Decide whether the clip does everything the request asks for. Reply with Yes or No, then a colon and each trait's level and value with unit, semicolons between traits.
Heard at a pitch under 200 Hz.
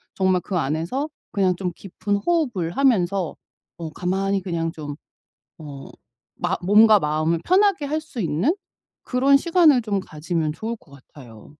Yes: high, 190 Hz